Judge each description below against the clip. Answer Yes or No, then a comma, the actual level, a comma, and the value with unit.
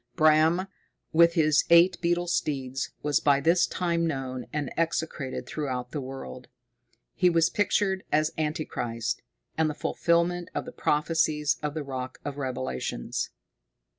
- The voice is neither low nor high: Yes, medium, 155 Hz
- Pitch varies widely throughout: No, average, 3.9 semitones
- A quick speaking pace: No, average, 140 wpm